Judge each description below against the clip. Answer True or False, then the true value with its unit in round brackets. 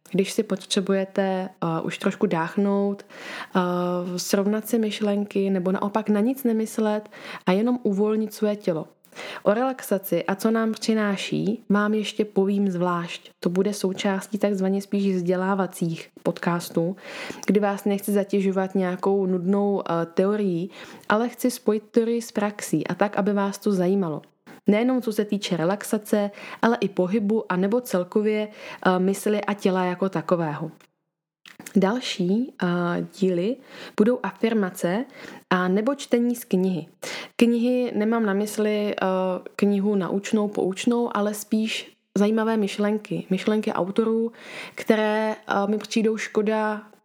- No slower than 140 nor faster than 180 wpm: False (130 wpm)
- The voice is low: False (205 Hz)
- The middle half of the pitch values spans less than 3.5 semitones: True (2.4 semitones)